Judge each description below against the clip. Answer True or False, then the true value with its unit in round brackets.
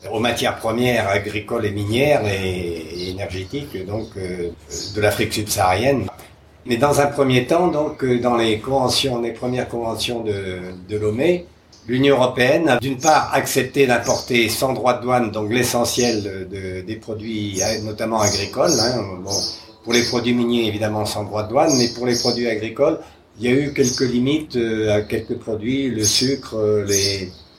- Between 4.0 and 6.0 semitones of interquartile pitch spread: False (3.2 semitones)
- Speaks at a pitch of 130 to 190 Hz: False (115 Hz)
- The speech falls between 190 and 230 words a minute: False (160 wpm)